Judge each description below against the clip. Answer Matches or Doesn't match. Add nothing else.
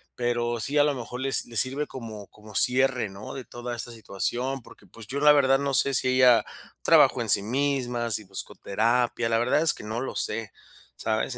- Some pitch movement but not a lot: Matches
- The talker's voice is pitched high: Doesn't match